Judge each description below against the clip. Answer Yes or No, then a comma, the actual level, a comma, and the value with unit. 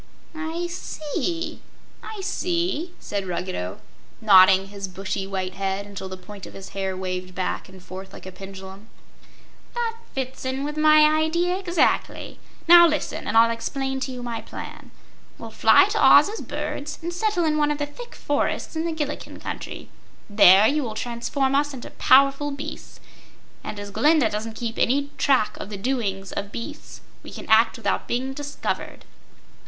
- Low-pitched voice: No, very high, 255 Hz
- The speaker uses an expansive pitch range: Yes, wide, 7.7 semitones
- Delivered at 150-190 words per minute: Yes, average, 170 wpm